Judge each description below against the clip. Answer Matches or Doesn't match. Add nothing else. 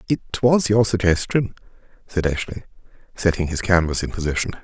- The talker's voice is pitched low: Matches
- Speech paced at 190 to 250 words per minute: Doesn't match